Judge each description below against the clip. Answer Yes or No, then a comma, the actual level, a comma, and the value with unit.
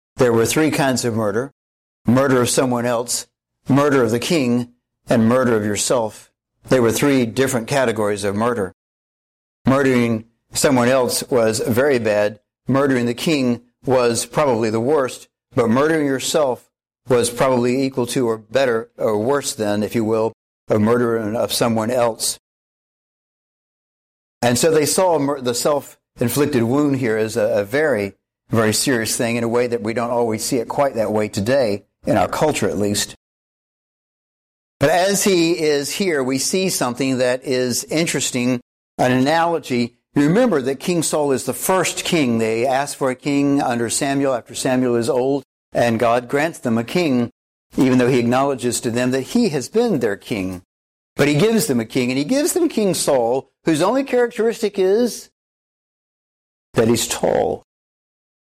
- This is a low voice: Yes, low, 125 Hz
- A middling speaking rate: Yes, average, 165 wpm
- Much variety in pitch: No, average, 3.6 semitones